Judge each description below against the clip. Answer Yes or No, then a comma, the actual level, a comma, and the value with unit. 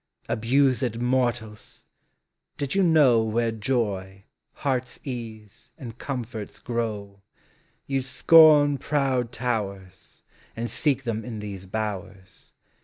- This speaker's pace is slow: Yes, slow, 110 wpm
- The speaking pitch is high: No, low, 115 Hz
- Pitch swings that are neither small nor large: Yes, average, 3.7 semitones